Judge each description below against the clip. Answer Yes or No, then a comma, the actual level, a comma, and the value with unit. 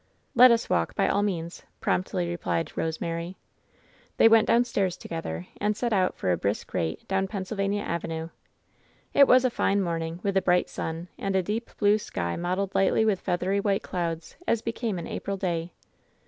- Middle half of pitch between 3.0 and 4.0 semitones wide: Yes, average, 3.5 semitones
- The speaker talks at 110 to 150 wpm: No, average, 175 wpm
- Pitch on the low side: No, high, 190 Hz